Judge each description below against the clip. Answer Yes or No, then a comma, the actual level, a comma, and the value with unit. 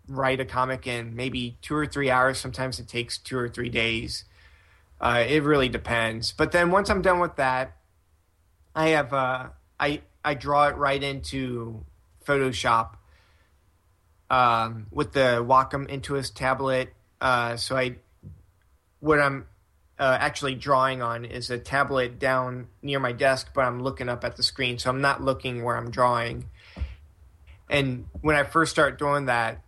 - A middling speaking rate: Yes, average, 160 wpm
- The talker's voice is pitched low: Yes, low, 125 Hz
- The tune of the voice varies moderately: Yes, average, 3.6 semitones